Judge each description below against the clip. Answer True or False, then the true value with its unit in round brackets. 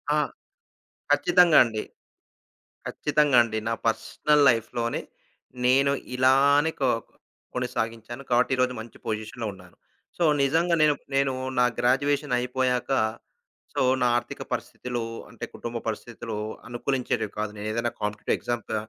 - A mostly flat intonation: False (3.4 semitones)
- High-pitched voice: False (125 Hz)